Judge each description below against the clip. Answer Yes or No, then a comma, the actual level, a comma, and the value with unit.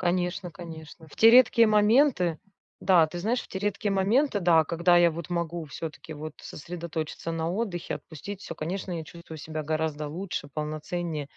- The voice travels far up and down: No, average, 3.3 semitones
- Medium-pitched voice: Yes, medium, 170 Hz